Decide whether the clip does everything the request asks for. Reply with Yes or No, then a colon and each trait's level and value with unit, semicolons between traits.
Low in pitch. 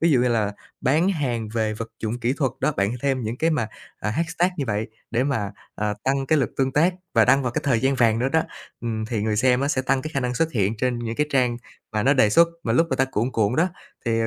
Yes: low, 125 Hz